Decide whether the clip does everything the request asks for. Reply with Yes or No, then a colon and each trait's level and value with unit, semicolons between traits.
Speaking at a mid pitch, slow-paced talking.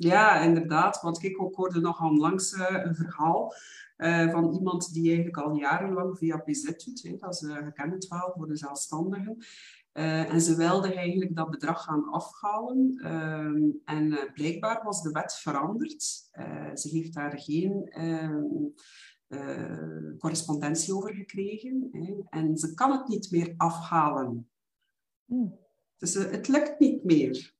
Yes: medium, 165 Hz; slow, 130 wpm